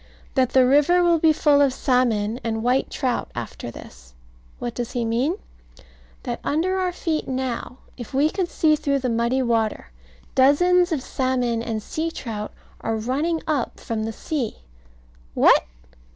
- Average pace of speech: Yes, average, 160 wpm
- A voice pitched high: Yes, very high, 260 Hz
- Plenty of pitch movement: No, average, 5.0 semitones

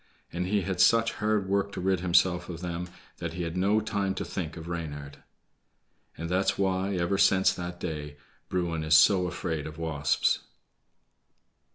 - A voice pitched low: Yes, very low, 90 Hz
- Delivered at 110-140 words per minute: No, average, 170 wpm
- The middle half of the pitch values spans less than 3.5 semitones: Yes, average, 2.7 semitones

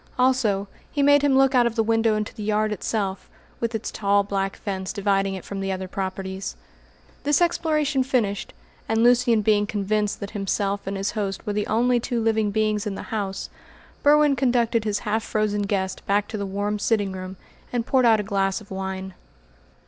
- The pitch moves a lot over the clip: No, average, 2.9 semitones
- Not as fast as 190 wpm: No, average, 195 wpm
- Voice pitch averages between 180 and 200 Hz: No, high, 210 Hz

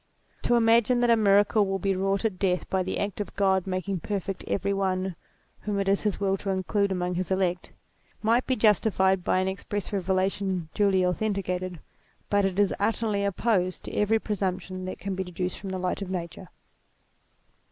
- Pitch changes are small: Yes, narrow, 1.7 semitones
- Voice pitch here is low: No, high, 195 Hz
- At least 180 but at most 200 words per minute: Yes, average, 185 wpm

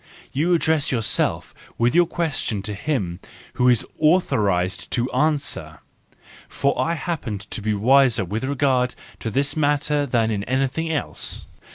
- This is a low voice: Yes, low, 130 Hz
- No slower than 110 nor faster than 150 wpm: Yes, average, 145 wpm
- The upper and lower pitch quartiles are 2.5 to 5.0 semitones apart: No, wide, 5.4 semitones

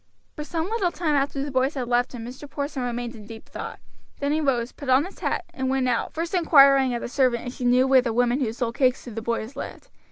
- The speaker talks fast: Yes, fast, 260 wpm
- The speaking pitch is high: Yes, very high, 260 Hz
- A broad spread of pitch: No, average, 2.8 semitones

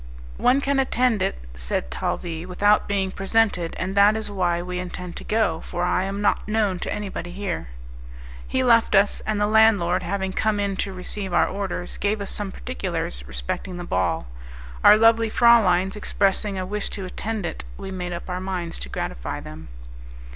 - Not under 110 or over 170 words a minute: No, average, 185 wpm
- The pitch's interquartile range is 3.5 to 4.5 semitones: No, average, 3.0 semitones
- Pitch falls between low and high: No, high, 195 Hz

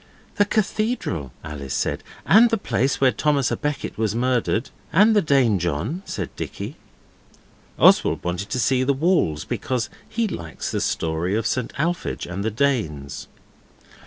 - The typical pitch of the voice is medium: No, low, 125 Hz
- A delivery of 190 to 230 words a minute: No, average, 150 wpm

